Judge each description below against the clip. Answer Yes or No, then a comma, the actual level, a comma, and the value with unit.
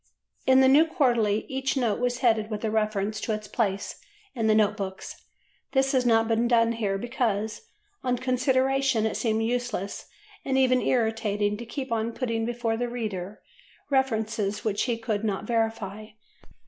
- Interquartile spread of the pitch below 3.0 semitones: Yes, narrow, 2.6 semitones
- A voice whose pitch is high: Yes, high, 225 Hz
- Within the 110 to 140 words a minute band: No, average, 165 wpm